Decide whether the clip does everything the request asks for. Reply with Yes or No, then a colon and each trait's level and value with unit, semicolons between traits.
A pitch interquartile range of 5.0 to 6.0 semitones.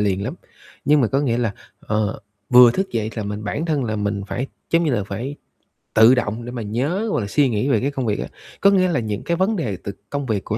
Yes: average, 5.3 semitones